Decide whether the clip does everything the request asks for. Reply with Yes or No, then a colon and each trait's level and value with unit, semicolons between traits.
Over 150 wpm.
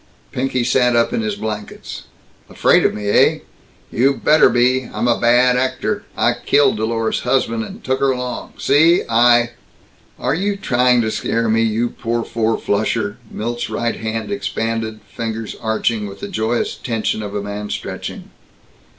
Yes: average, 165 wpm